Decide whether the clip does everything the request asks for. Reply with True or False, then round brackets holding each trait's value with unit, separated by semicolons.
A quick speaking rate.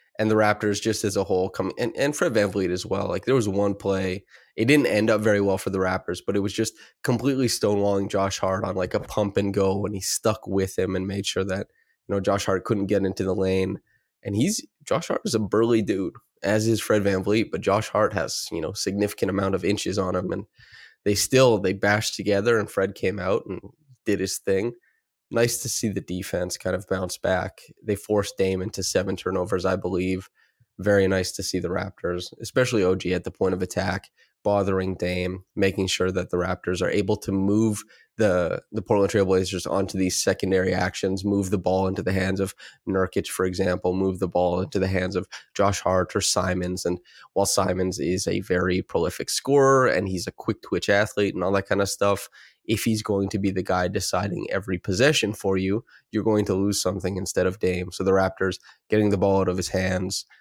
True (220 wpm)